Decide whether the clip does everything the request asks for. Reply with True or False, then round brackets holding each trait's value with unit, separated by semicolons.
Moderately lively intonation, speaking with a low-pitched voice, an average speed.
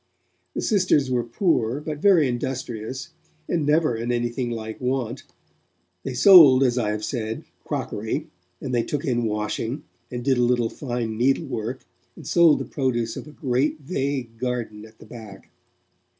True (3.2 semitones; 125 Hz; 160 wpm)